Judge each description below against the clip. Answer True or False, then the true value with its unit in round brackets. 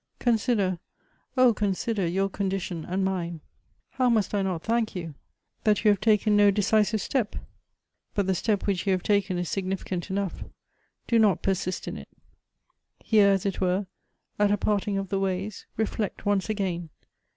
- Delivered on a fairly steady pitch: True (2.2 semitones)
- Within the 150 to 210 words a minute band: True (170 wpm)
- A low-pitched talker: False (195 Hz)